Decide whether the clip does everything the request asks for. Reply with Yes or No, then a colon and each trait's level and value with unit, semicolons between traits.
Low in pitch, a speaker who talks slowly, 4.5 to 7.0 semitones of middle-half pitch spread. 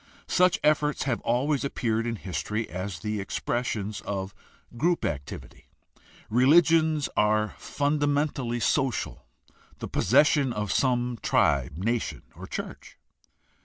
Yes: low, 120 Hz; slow, 115 wpm; wide, 5.6 semitones